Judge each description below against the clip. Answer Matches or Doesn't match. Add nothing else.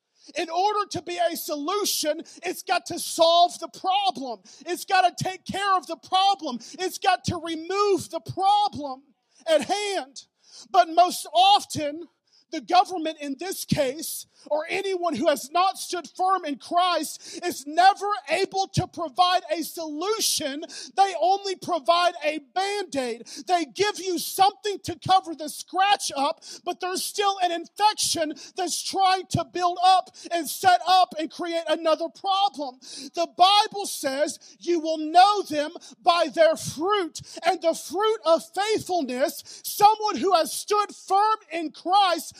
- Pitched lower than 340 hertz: Doesn't match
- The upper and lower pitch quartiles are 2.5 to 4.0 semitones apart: Matches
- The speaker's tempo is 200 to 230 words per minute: Doesn't match